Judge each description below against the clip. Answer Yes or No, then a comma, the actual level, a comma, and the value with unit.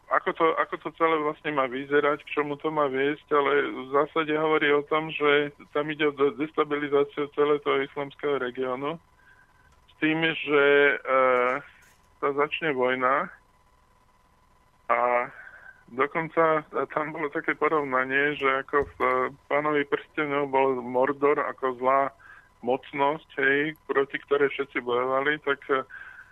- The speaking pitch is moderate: Yes, medium, 145 Hz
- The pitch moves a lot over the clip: No, narrow, 2.4 semitones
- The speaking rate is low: No, average, 130 wpm